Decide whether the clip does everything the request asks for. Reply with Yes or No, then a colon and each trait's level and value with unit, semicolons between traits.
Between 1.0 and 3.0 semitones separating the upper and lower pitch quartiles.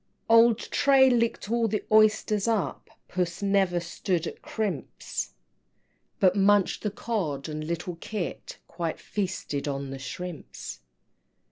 No: average, 4.4 semitones